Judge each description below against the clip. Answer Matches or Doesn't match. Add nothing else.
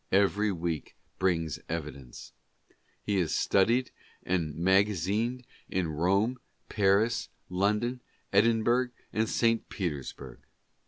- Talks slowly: Matches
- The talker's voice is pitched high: Doesn't match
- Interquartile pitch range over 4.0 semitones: Matches